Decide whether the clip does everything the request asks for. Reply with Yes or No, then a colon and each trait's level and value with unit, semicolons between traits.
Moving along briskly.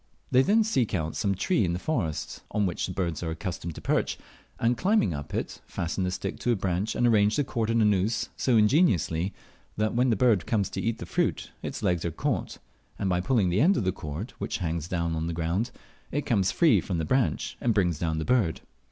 Yes: fast, 235 wpm